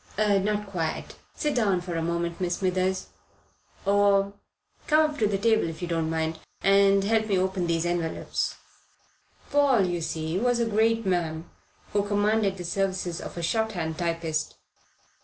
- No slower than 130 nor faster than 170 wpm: Yes, average, 160 wpm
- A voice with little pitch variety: No, average, 3.6 semitones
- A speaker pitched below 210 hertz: Yes, high, 190 Hz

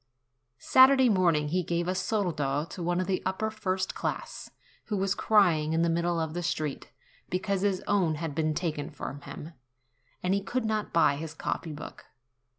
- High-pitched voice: No, medium, 175 Hz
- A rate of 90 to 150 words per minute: No, average, 180 wpm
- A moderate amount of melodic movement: Yes, average, 3.6 semitones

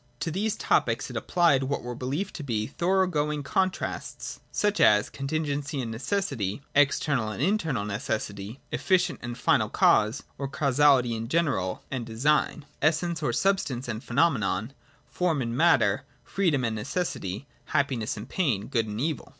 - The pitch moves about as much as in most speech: No, wide, 6.2 semitones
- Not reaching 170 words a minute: Yes, average, 155 wpm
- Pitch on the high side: No, medium, 140 Hz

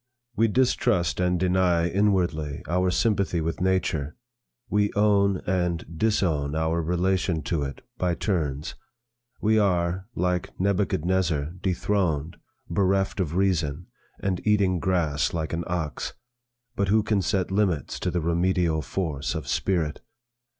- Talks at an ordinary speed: No, slow, 130 wpm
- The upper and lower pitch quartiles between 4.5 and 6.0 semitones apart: No, average, 3.0 semitones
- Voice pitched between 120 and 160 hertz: No, very low, 90 Hz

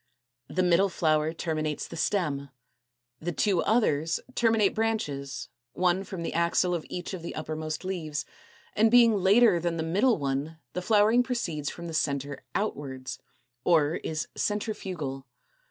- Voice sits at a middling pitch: Yes, medium, 170 Hz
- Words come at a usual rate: Yes, average, 155 wpm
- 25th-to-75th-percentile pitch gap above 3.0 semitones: Yes, average, 4.8 semitones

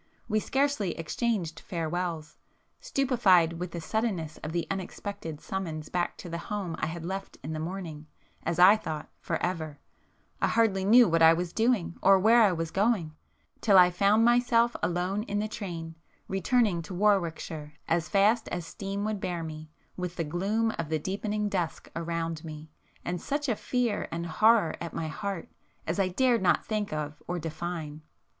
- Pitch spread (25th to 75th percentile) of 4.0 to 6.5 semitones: Yes, average, 4.3 semitones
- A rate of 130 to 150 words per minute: No, average, 175 wpm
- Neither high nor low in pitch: Yes, medium, 180 Hz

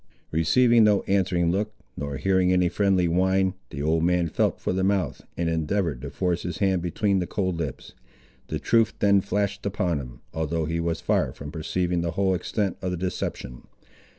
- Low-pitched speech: Yes, very low, 90 Hz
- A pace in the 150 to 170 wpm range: No, average, 185 wpm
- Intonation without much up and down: No, average, 3.0 semitones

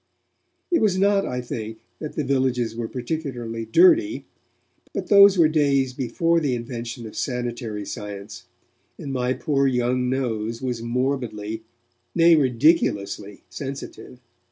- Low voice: Yes, low, 125 Hz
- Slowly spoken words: Yes, slow, 130 wpm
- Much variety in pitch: No, average, 4.5 semitones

